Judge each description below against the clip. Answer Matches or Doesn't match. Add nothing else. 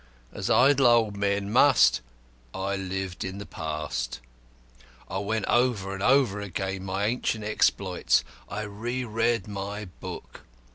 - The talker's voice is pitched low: Matches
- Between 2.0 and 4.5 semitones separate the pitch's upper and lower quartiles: Matches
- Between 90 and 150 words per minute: Matches